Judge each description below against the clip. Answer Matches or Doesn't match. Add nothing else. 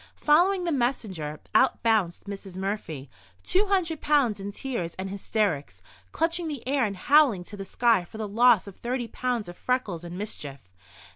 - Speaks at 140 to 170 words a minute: Matches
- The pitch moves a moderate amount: Doesn't match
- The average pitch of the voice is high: Matches